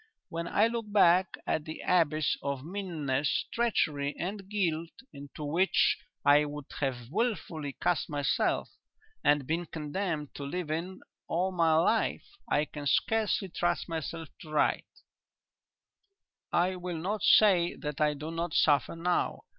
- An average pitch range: Yes, average, 3.8 semitones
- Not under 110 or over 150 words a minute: Yes, average, 140 wpm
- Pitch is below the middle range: No, medium, 165 Hz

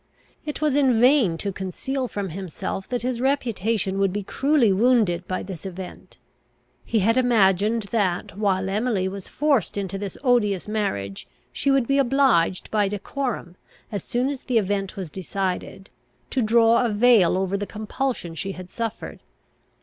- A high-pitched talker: Yes, high, 210 Hz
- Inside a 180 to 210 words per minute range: No, average, 160 wpm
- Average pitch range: Yes, average, 4.5 semitones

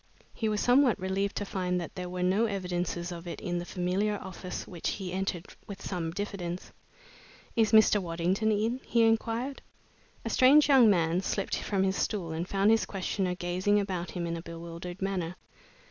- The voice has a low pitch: No, high, 190 Hz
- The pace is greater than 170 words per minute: Yes, average, 180 wpm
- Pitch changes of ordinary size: Yes, average, 3.0 semitones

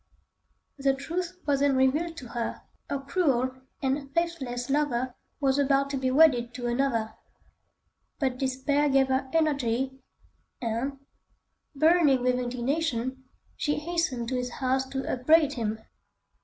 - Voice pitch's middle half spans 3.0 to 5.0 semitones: No, narrow, 2.5 semitones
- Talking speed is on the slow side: Yes, slow, 130 wpm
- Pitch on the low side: No, very high, 270 Hz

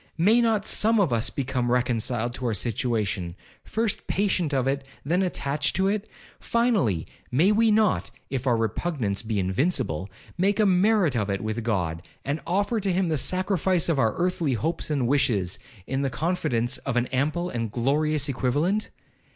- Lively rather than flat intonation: Yes, wide, 7.8 semitones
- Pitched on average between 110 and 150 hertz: Yes, medium, 140 Hz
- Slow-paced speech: No, average, 165 wpm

